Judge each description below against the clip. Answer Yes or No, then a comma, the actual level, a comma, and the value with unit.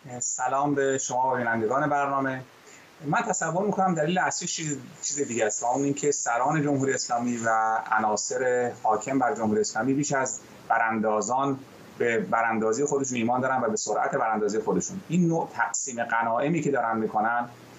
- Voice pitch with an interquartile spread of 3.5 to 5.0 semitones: Yes, average, 4.1 semitones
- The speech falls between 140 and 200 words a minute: Yes, average, 150 wpm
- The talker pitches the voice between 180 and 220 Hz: No, low, 130 Hz